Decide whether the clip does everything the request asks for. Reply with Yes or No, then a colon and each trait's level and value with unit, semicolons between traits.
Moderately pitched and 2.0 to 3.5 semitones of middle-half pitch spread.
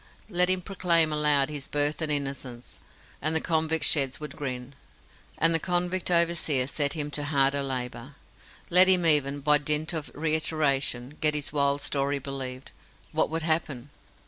Yes: medium, 150 Hz; narrow, 2.6 semitones